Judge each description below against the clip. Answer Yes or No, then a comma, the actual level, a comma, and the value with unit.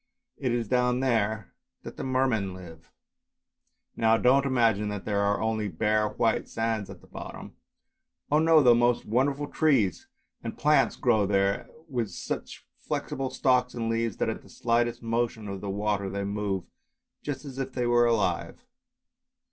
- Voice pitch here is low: Yes, low, 115 Hz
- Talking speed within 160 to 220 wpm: Yes, average, 165 wpm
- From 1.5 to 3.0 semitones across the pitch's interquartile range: No, average, 3.6 semitones